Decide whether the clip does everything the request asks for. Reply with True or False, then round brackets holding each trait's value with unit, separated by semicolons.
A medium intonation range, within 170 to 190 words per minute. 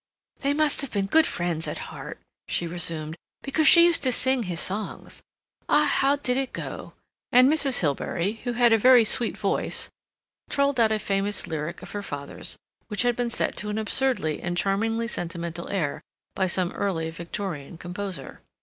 False (6.5 semitones; 175 wpm)